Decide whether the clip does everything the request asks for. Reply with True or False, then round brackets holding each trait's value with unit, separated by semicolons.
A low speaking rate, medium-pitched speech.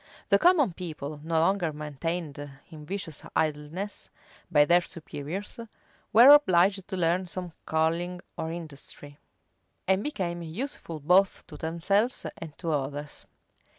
True (125 wpm; 170 Hz)